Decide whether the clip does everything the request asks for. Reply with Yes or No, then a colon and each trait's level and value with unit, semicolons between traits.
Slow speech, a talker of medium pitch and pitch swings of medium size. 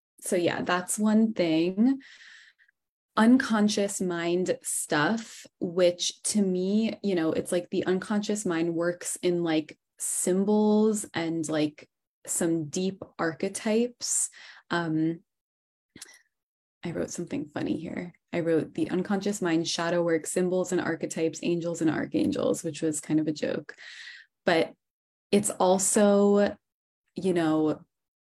Yes: slow, 120 wpm; medium, 180 Hz; average, 4.0 semitones